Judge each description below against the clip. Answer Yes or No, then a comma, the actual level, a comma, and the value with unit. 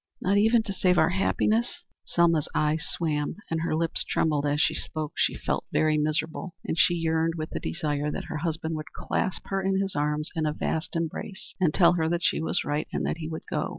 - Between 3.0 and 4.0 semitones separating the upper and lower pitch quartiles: No, narrow, 2.6 semitones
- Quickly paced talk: Yes, fast, 220 wpm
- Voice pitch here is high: No, medium, 160 Hz